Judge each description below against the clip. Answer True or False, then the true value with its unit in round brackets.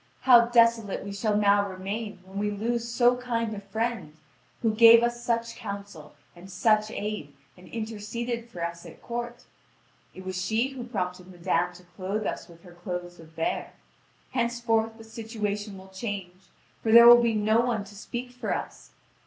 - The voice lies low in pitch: False (215 Hz)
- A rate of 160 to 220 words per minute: True (175 wpm)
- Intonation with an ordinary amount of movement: True (3.8 semitones)